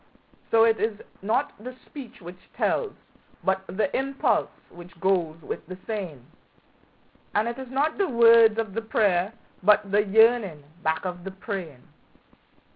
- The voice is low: No, high, 210 Hz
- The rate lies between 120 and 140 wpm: No, average, 150 wpm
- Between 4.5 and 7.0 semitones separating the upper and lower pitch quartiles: No, average, 4.1 semitones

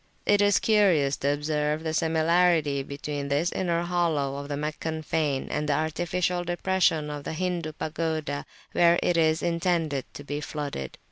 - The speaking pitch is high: No, medium, 155 Hz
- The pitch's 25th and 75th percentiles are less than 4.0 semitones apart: Yes, average, 2.9 semitones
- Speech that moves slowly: No, average, 160 wpm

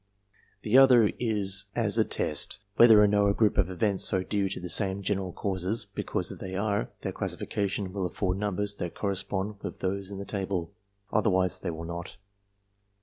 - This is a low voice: Yes, low, 100 Hz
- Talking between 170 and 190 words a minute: Yes, average, 185 wpm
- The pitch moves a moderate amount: No, narrow, 1.8 semitones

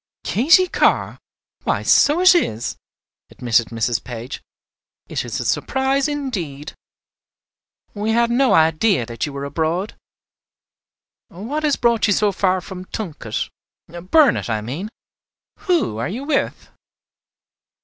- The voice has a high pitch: Yes, high, 195 Hz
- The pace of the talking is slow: Yes, slow, 125 wpm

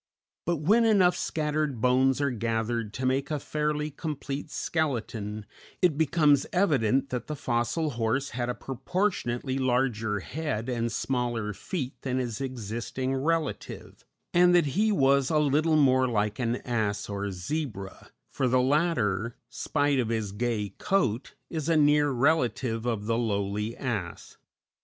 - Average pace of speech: Yes, average, 145 wpm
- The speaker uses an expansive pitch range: No, average, 4.7 semitones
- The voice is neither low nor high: No, low, 130 Hz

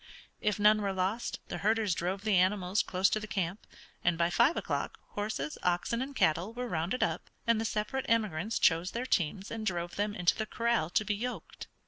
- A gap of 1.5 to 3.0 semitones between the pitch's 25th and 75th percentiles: No, average, 3.9 semitones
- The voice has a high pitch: Yes, high, 205 Hz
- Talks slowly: No, average, 200 wpm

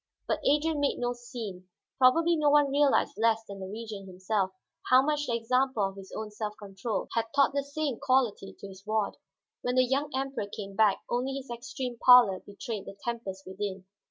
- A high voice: Yes, high, 235 Hz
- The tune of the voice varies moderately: Yes, average, 5.0 semitones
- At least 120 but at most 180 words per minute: No, average, 190 wpm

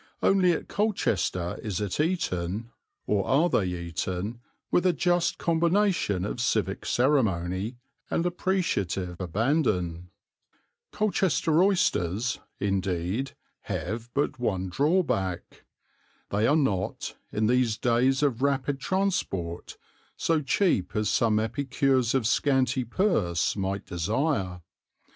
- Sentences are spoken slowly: Yes, slow, 110 wpm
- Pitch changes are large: Yes, wide, 8.3 semitones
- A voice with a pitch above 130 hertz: No, low, 120 Hz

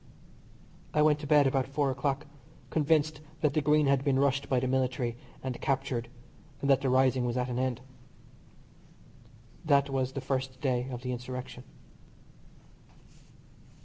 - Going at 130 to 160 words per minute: Yes, average, 150 wpm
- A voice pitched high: No, low, 135 Hz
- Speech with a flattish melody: Yes, narrow, 1.8 semitones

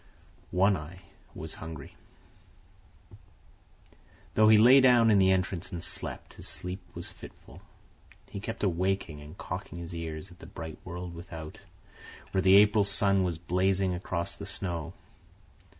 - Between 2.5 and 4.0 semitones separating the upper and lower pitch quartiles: Yes, average, 2.8 semitones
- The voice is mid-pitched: No, very low, 95 Hz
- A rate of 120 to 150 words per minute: Yes, average, 145 wpm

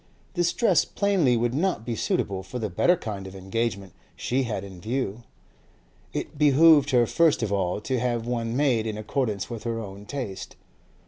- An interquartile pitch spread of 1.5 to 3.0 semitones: No, average, 5.2 semitones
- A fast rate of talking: No, average, 180 wpm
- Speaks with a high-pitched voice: No, low, 115 Hz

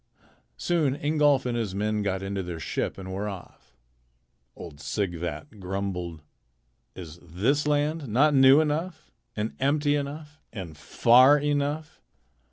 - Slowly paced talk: Yes, slow, 130 wpm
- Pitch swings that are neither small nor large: No, wide, 7.7 semitones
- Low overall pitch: Yes, low, 120 Hz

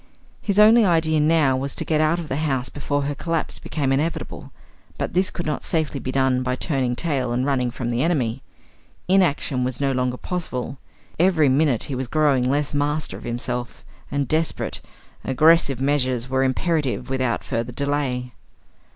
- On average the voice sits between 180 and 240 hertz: No, medium, 140 Hz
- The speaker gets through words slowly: No, average, 170 wpm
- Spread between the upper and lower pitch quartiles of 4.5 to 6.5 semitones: No, average, 3.5 semitones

